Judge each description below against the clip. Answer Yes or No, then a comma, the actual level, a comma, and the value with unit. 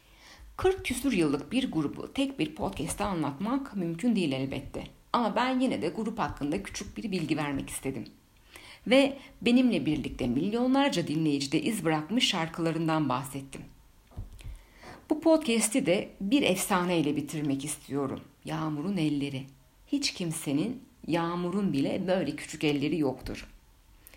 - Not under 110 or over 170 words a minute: Yes, average, 120 wpm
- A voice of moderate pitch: Yes, medium, 165 Hz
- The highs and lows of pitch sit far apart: Yes, wide, 8.9 semitones